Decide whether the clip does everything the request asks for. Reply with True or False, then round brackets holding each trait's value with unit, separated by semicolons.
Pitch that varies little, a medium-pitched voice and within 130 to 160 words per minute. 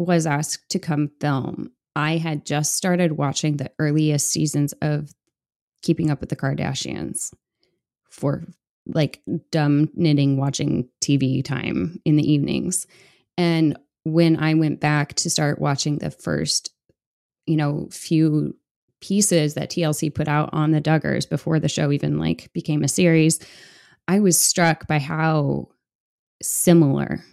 True (2.1 semitones; 155 Hz; 140 wpm)